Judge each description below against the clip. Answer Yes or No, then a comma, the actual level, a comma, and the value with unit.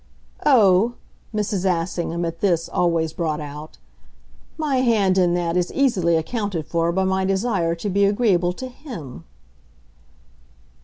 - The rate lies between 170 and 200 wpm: No, slow, 135 wpm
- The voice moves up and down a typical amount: Yes, average, 3.8 semitones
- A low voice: No, medium, 180 Hz